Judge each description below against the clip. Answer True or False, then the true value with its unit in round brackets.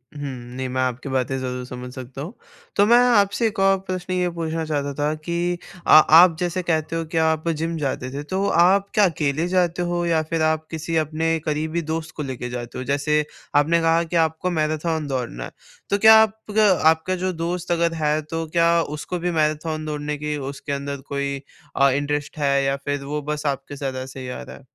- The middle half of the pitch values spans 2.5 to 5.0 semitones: True (3.2 semitones)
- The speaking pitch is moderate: True (155 Hz)